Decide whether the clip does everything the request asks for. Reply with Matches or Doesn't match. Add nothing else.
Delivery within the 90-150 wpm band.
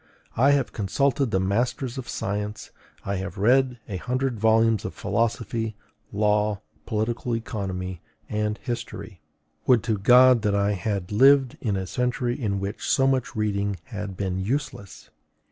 Matches